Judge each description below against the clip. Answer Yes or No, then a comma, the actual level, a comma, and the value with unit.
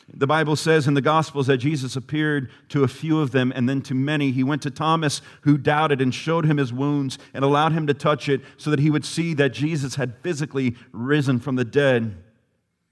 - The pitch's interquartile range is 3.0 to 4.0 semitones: No, narrow, 2.4 semitones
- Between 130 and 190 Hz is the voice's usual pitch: Yes, medium, 140 Hz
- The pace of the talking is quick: Yes, fast, 225 wpm